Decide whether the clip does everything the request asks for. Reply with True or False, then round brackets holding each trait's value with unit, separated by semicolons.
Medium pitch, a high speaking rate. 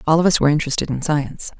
True (150 Hz; 265 wpm)